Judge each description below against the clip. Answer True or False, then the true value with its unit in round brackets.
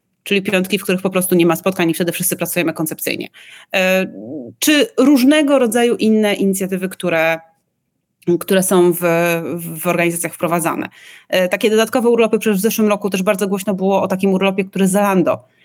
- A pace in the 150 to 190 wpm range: True (160 wpm)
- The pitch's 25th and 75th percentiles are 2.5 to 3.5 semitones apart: True (3.1 semitones)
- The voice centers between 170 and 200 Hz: True (190 Hz)